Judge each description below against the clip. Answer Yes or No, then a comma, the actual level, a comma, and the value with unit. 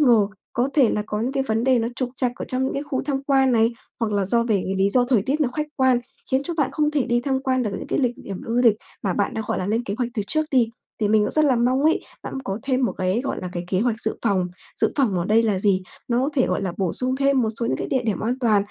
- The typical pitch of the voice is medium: No, high, 240 Hz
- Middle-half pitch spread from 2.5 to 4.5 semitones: Yes, average, 4.0 semitones